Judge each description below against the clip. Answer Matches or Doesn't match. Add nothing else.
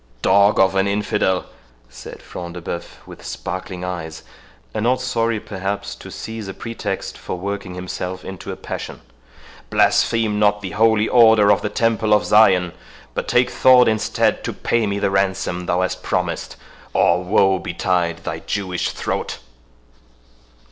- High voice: Doesn't match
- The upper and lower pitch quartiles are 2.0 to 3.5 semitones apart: Matches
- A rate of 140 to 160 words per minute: Matches